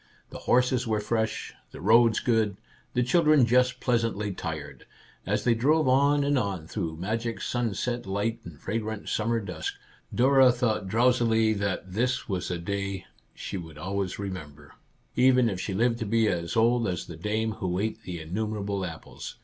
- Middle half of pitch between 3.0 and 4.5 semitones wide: Yes, average, 4.2 semitones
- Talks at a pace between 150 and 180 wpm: Yes, average, 170 wpm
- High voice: No, low, 110 Hz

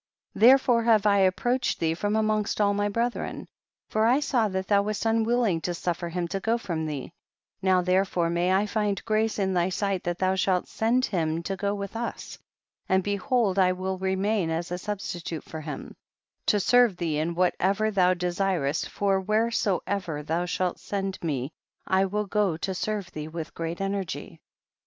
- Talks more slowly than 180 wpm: No, average, 185 wpm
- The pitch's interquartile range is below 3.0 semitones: No, average, 3.3 semitones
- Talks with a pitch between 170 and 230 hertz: Yes, high, 190 Hz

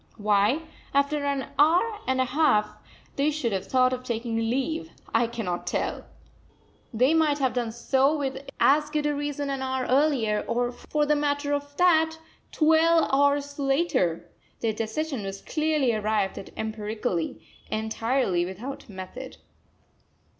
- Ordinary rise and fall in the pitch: Yes, average, 4.7 semitones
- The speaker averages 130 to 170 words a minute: Yes, average, 145 wpm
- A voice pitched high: Yes, very high, 265 Hz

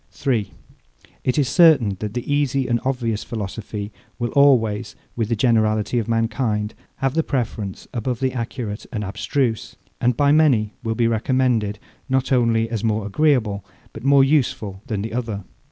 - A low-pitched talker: Yes, low, 115 Hz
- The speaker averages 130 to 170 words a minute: Yes, average, 160 wpm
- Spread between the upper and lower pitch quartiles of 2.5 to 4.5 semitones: Yes, average, 3.4 semitones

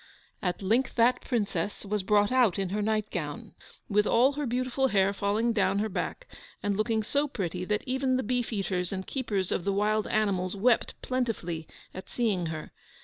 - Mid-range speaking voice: No, high, 210 Hz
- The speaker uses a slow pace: No, average, 180 wpm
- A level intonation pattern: No, average, 4.0 semitones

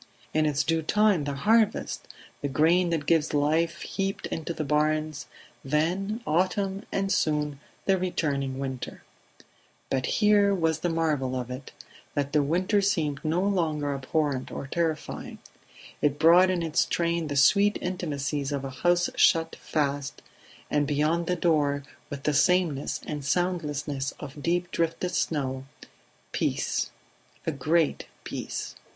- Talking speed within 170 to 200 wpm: No, average, 145 wpm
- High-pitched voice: No, medium, 155 Hz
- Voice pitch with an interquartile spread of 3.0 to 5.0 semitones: Yes, average, 3.6 semitones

